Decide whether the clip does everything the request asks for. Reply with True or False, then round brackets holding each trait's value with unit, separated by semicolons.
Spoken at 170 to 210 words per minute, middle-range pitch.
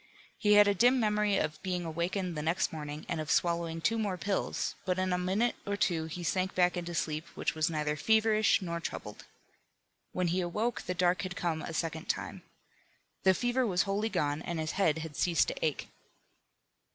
True (200 wpm; 180 Hz)